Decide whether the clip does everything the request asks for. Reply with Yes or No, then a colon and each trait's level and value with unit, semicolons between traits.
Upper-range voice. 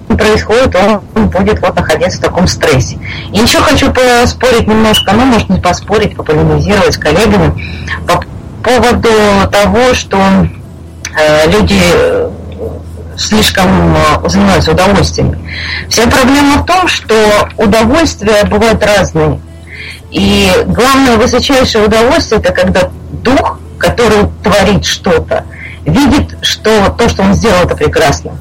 Yes: high, 205 Hz